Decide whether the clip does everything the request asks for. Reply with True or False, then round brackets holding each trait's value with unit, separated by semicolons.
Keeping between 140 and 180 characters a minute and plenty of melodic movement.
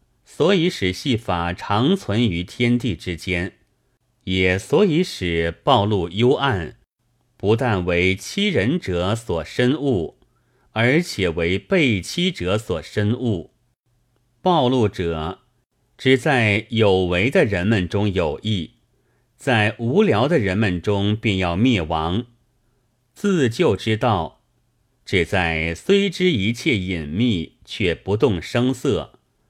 False (160 characters per minute; 5.0 semitones)